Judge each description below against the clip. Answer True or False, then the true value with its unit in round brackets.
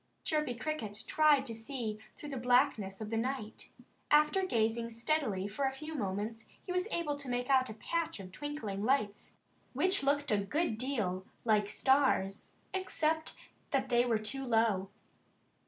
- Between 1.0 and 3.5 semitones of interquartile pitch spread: False (5.3 semitones)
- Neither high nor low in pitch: False (245 Hz)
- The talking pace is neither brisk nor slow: True (160 wpm)